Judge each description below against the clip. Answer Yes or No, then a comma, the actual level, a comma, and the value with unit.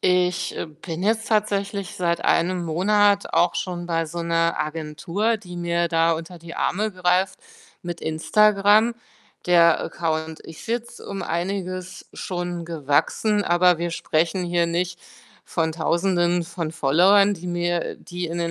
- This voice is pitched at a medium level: Yes, medium, 175 Hz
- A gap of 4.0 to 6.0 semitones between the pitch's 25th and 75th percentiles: No, narrow, 2.6 semitones